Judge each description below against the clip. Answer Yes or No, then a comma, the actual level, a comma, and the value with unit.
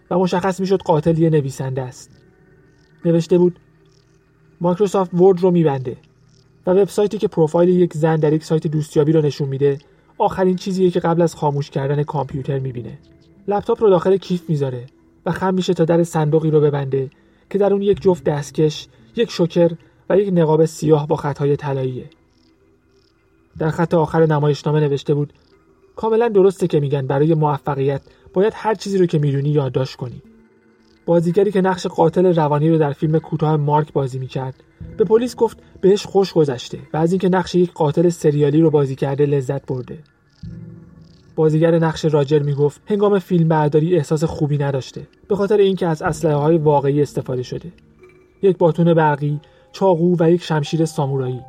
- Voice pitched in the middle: Yes, medium, 160 Hz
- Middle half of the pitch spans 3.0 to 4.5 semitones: Yes, average, 3.9 semitones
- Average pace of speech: No, fast, 160 wpm